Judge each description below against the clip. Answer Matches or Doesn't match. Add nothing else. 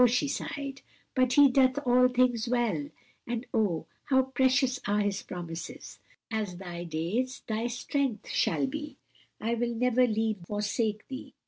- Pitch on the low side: Doesn't match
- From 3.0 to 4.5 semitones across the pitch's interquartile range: Matches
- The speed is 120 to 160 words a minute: Matches